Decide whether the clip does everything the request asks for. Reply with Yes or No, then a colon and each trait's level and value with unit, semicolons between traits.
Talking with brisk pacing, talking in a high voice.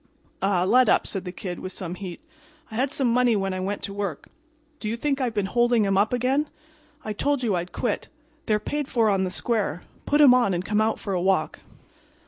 Yes: fast, 230 wpm; high, 210 Hz